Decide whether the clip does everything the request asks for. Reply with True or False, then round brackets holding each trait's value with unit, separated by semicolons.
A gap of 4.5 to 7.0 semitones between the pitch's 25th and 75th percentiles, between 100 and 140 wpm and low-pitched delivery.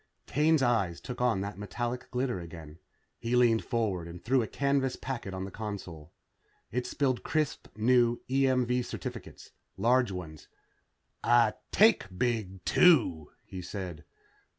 True (5.2 semitones; 135 wpm; 115 Hz)